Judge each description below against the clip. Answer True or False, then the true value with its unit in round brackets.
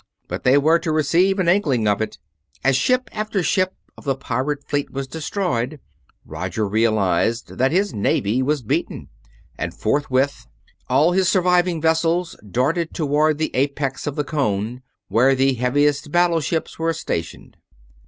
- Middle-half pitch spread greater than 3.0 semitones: True (4.7 semitones)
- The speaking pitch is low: False (145 Hz)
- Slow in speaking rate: False (150 wpm)